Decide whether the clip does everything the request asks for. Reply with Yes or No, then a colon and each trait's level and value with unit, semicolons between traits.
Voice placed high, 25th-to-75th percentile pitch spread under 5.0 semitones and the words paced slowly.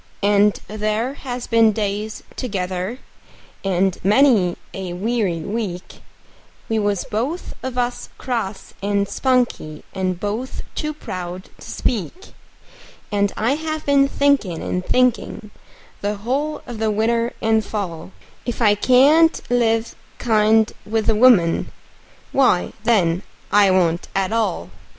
Yes: high, 215 Hz; average, 4.1 semitones; slow, 125 wpm